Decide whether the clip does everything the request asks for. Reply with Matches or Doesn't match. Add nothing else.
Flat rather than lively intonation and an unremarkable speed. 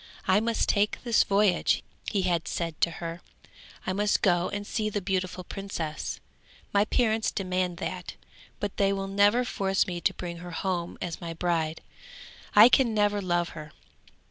Doesn't match